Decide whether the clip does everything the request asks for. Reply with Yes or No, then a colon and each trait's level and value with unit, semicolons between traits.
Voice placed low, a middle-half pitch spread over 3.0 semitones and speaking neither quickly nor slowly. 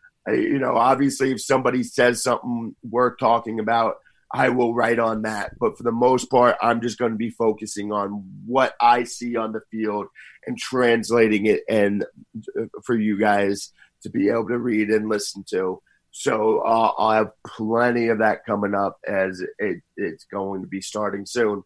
No: low, 115 Hz; narrow, 2.6 semitones; average, 185 wpm